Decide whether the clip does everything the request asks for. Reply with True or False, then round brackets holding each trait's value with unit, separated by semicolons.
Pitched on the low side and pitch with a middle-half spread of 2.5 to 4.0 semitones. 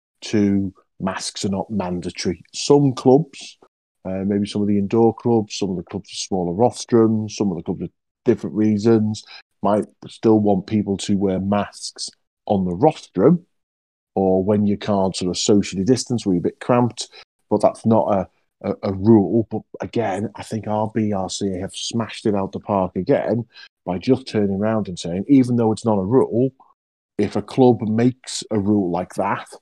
True (105 Hz; 3.0 semitones)